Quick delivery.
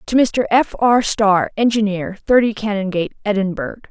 No: average, 140 wpm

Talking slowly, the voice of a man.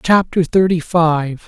Yes: slow, 120 wpm; male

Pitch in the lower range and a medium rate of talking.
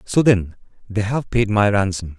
Yes: low, 105 Hz; average, 190 wpm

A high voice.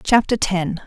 Yes: high, 195 Hz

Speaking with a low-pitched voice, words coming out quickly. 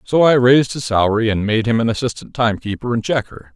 Yes: low, 115 Hz; fast, 220 wpm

